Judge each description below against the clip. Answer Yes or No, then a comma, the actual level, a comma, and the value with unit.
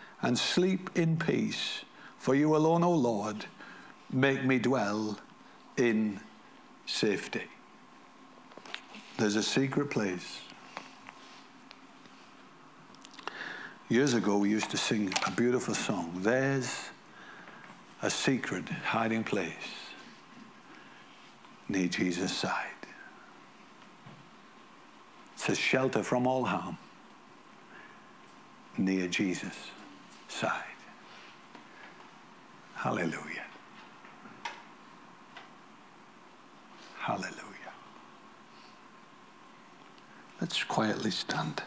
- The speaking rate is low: Yes, slow, 70 wpm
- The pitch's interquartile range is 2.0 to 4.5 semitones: Yes, average, 4.2 semitones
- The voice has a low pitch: Yes, low, 125 Hz